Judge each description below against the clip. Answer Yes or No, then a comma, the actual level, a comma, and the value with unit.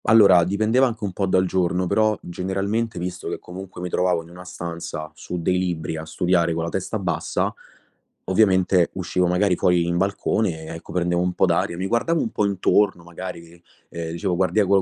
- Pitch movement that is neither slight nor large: No, narrow, 2.3 semitones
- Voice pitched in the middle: No, very low, 90 Hz